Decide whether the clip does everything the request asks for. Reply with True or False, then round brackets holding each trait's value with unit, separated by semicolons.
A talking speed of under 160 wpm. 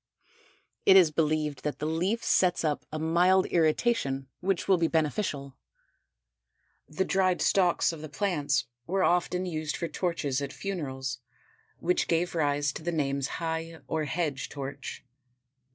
True (145 wpm)